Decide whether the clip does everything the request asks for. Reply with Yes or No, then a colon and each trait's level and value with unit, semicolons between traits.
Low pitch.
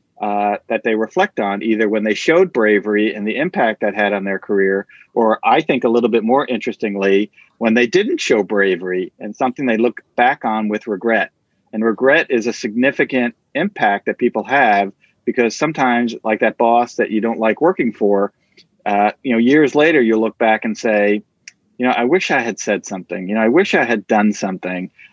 Yes: low, 110 Hz